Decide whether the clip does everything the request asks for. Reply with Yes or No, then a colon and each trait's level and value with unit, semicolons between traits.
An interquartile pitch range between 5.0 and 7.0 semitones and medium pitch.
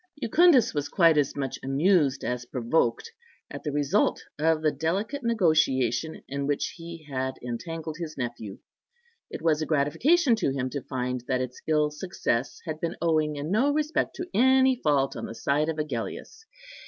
No: average, 4.2 semitones; medium, 155 Hz